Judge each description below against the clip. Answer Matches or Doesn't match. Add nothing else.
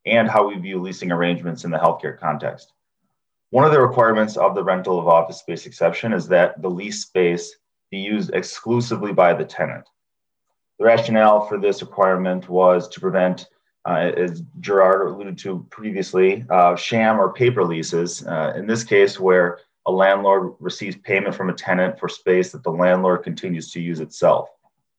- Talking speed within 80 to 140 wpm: Doesn't match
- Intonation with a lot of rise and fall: Doesn't match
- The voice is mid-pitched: Doesn't match